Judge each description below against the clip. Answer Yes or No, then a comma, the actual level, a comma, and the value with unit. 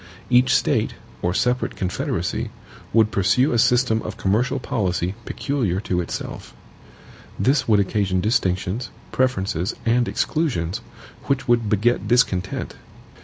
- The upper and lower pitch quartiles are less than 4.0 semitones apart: No, average, 4.8 semitones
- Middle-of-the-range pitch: No, low, 110 Hz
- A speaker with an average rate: No, slow, 120 wpm